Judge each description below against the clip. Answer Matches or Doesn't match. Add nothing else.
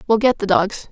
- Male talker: Doesn't match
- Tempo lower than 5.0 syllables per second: Doesn't match